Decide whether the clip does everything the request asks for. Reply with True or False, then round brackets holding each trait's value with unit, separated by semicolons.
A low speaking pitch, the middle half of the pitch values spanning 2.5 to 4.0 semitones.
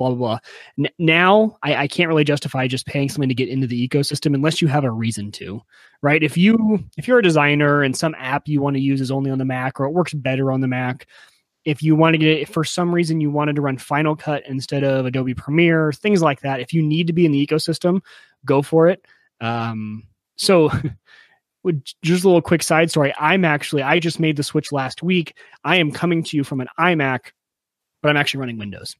False (145 Hz; 3.5 semitones)